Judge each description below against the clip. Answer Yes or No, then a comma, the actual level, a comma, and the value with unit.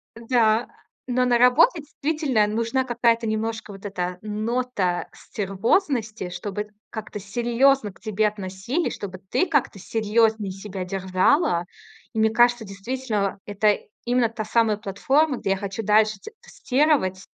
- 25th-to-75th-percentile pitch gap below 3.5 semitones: No, average, 3.8 semitones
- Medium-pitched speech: No, high, 220 Hz